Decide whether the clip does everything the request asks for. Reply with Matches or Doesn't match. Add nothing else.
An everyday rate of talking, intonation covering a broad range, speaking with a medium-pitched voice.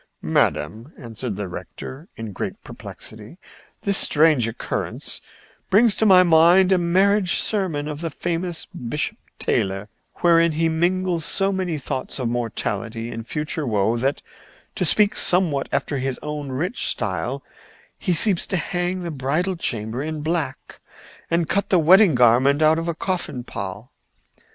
Matches